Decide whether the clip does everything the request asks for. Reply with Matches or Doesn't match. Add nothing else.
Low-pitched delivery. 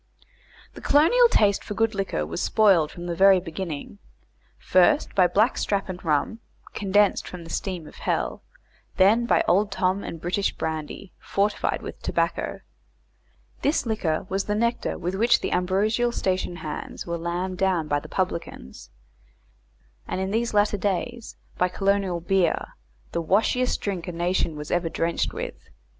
Doesn't match